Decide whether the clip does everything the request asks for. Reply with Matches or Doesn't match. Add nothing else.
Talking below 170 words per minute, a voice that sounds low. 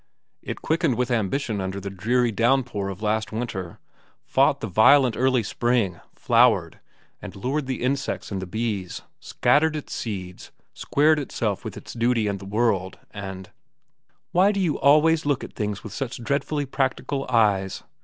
Matches